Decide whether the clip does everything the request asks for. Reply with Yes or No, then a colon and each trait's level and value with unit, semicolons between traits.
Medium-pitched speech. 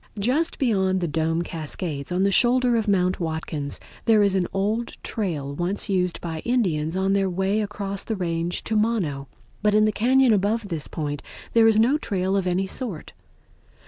No: high, 195 Hz